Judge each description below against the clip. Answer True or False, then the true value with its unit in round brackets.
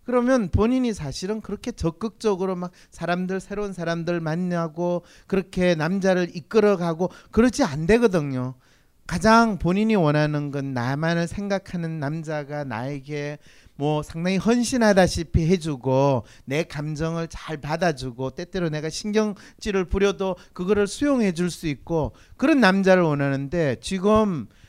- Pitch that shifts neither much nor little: True (4.9 semitones)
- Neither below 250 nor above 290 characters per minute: False (305 characters per minute)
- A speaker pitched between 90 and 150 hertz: False (175 Hz)